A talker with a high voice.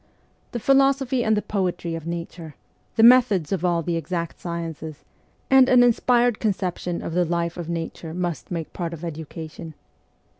No: medium, 175 Hz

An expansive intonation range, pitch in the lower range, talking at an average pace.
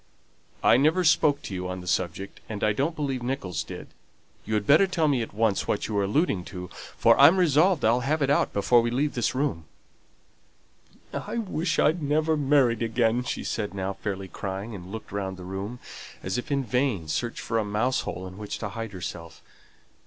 Yes: wide, 6.5 semitones; low, 115 Hz; average, 195 wpm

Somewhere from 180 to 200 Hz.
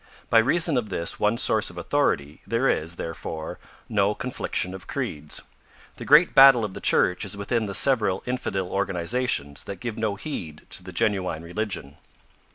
No: low, 100 Hz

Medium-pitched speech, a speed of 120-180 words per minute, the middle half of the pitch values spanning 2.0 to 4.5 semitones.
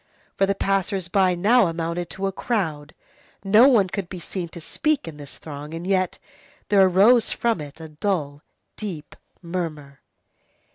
Yes: medium, 180 Hz; average, 160 wpm; average, 3.5 semitones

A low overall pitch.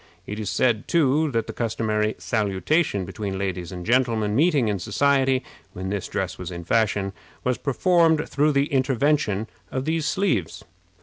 Yes: low, 115 Hz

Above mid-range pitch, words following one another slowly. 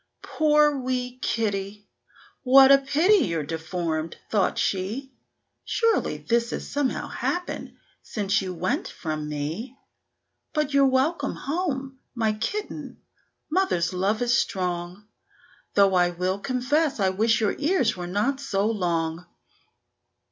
Yes: high, 220 Hz; slow, 125 wpm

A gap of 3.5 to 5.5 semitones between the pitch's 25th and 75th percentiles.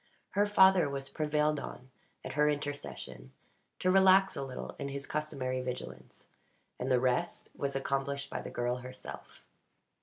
No: average, 3.0 semitones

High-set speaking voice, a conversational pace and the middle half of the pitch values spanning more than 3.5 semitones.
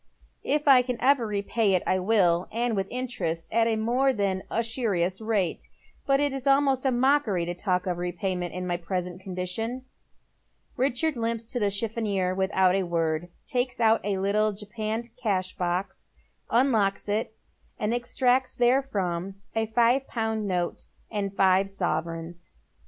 Yes: high, 210 Hz; average, 155 wpm; average, 4.7 semitones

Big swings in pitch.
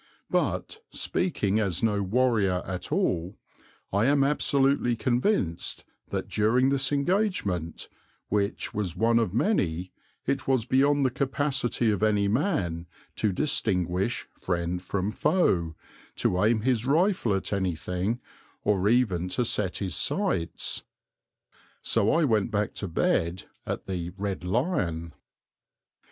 Yes: wide, 6.3 semitones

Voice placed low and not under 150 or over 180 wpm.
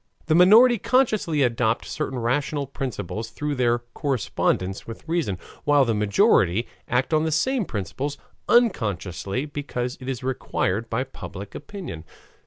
No: low, 130 Hz; slow, 135 wpm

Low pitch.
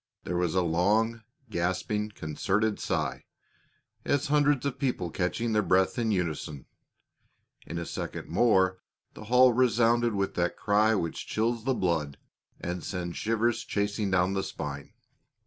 Yes: low, 100 Hz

